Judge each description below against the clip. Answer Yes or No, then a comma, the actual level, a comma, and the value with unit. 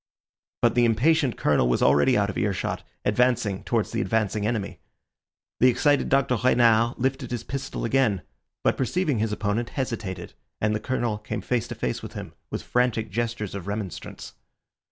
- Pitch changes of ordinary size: Yes, average, 3.3 semitones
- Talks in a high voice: No, low, 115 Hz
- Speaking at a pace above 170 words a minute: No, average, 165 wpm